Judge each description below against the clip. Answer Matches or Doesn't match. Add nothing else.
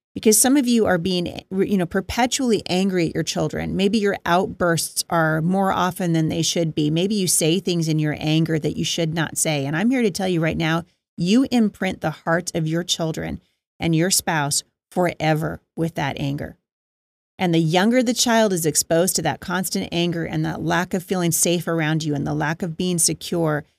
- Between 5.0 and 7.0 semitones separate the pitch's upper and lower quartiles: Doesn't match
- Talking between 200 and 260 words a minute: Matches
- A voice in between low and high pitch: Matches